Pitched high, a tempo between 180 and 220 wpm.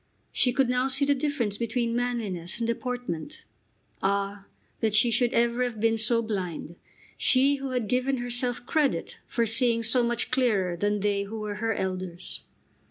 No: high, 235 Hz; average, 165 wpm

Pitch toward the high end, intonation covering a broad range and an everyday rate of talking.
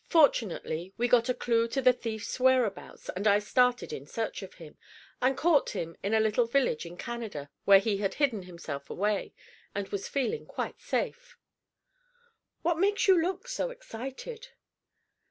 Yes: high, 230 Hz; wide, 5.9 semitones; average, 165 wpm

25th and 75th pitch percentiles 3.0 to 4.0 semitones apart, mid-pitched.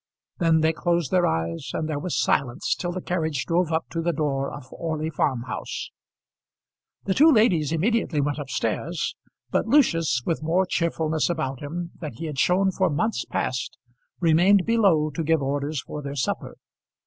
Yes: average, 3.5 semitones; medium, 160 Hz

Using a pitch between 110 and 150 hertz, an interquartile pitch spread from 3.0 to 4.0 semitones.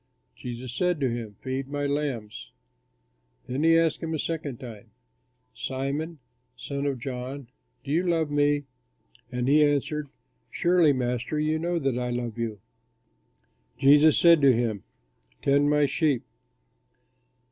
Yes: medium, 140 Hz; average, 3.6 semitones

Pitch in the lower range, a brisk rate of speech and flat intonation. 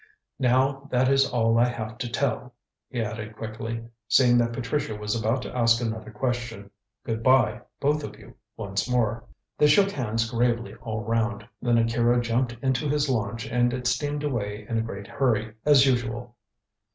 No: low, 120 Hz; average, 175 wpm; narrow, 2.3 semitones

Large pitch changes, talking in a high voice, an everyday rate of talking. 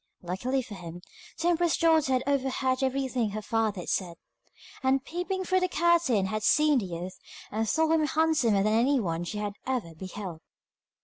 Yes: wide, 7.3 semitones; very high, 255 Hz; average, 175 wpm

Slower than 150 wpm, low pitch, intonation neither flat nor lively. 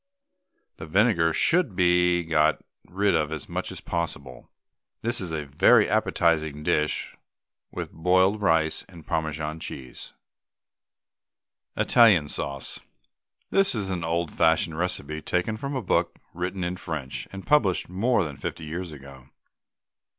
Yes: slow, 135 wpm; very low, 85 Hz; average, 3.4 semitones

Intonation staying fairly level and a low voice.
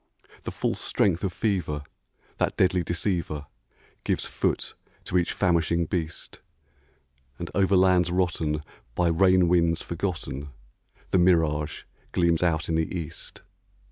Yes: narrow, 2.1 semitones; very low, 85 Hz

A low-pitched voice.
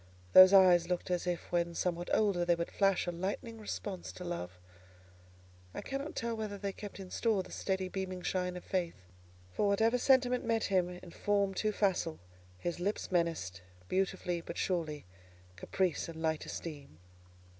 No: medium, 185 Hz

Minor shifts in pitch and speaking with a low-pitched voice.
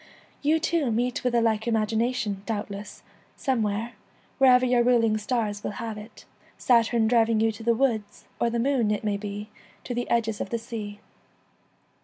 No: narrow, 2.3 semitones; high, 230 Hz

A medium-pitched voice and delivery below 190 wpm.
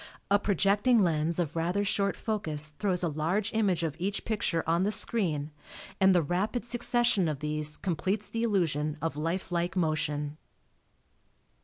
Yes: medium, 175 Hz; average, 155 wpm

